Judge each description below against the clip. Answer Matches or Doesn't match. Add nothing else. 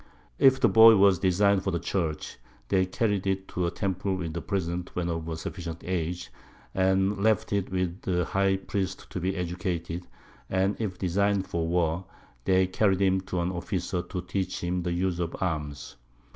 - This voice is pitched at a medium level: Doesn't match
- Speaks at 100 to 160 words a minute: Doesn't match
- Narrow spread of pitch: Matches